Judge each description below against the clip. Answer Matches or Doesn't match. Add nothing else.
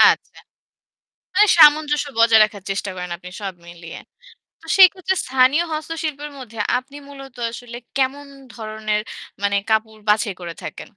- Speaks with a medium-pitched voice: Doesn't match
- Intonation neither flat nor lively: Doesn't match